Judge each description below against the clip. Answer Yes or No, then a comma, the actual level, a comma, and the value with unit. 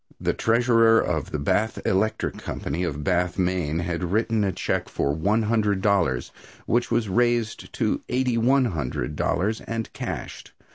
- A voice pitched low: Yes, low, 100 Hz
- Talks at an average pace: Yes, average, 155 wpm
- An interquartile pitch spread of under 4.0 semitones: No, average, 4.9 semitones